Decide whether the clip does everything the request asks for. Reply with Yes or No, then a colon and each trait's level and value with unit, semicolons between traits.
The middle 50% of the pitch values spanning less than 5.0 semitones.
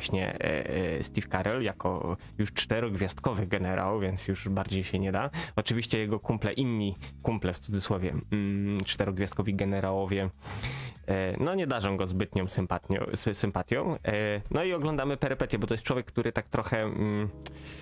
Yes: average, 3.1 semitones